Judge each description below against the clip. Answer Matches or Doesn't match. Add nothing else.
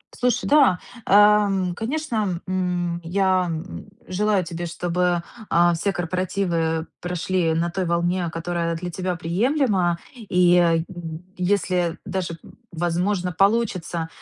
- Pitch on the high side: Doesn't match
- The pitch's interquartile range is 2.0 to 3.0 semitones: Matches